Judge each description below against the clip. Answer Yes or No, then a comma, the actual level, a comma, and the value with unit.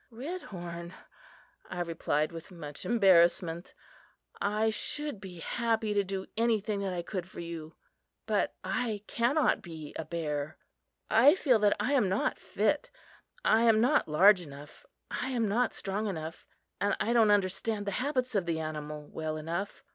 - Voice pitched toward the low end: No, high, 195 Hz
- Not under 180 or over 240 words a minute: No, average, 155 wpm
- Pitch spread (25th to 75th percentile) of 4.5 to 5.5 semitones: Yes, average, 5.1 semitones